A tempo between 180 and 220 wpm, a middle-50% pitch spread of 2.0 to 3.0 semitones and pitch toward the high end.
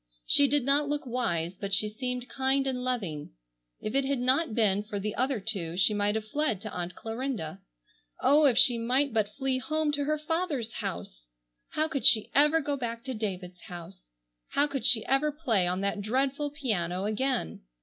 No: average, 190 wpm; wide, 5.4 semitones; high, 240 Hz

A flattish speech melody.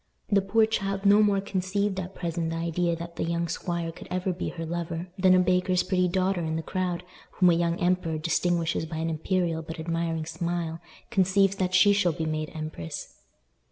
Yes: narrow, 2.2 semitones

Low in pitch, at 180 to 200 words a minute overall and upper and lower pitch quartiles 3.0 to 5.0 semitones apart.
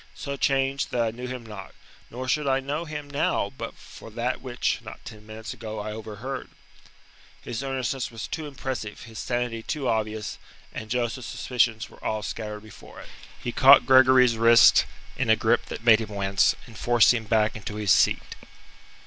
Yes: low, 120 Hz; average, 185 wpm; average, 3.3 semitones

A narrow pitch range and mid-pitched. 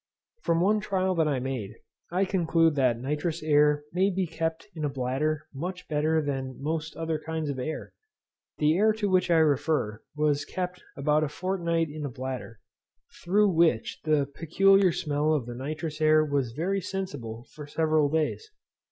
No: average, 3.2 semitones; medium, 155 Hz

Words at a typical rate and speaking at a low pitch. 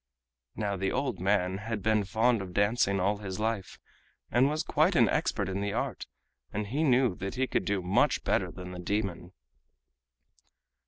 Yes: average, 175 wpm; low, 105 Hz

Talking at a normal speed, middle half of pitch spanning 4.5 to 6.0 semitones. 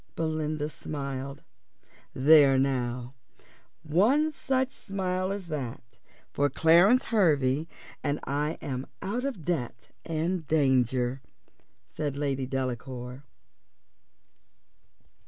No: slow, 85 wpm; average, 4.9 semitones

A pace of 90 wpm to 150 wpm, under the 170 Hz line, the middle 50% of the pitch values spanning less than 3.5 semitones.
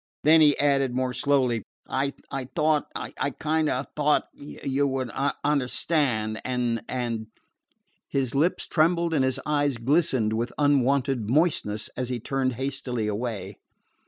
Yes: average, 140 wpm; low, 135 Hz; average, 3.0 semitones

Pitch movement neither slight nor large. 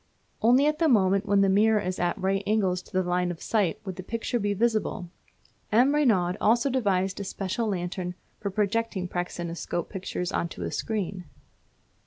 Yes: average, 3.6 semitones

